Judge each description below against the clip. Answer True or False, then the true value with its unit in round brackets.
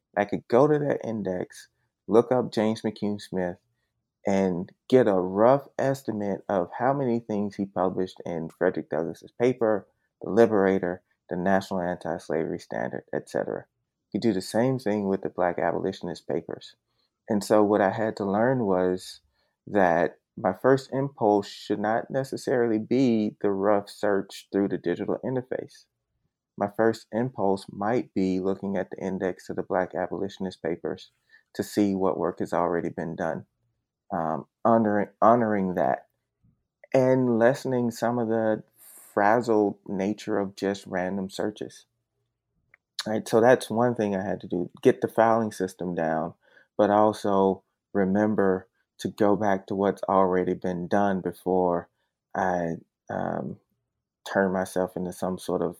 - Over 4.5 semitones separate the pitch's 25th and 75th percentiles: False (3.3 semitones)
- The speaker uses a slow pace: False (150 wpm)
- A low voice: True (100 Hz)